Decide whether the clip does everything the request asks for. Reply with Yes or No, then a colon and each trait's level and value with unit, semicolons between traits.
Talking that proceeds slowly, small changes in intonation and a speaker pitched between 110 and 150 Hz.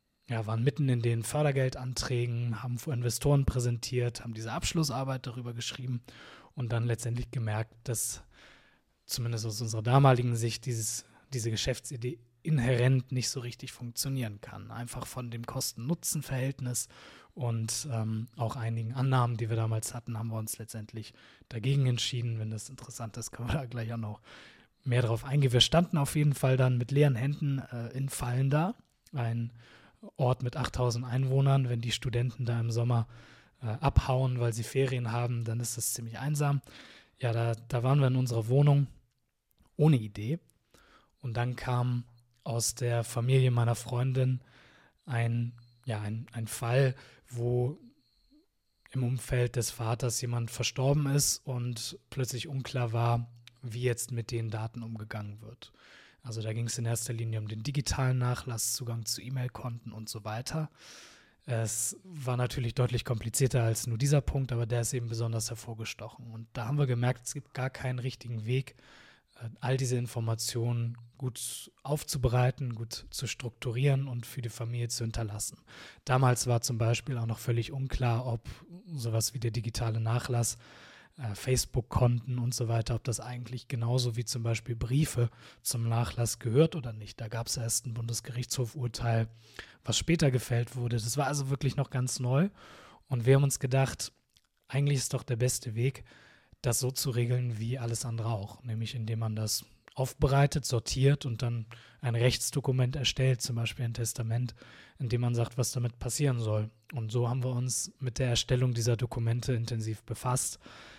No: average, 165 wpm; narrow, 2.0 semitones; low, 120 Hz